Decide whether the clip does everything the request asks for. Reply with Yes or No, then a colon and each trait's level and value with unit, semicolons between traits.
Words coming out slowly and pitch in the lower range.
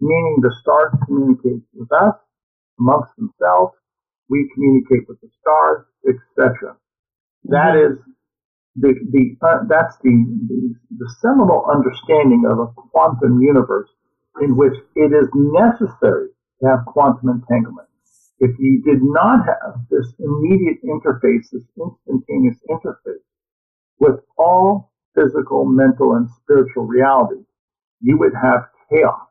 No: slow, 125 wpm; medium, 145 Hz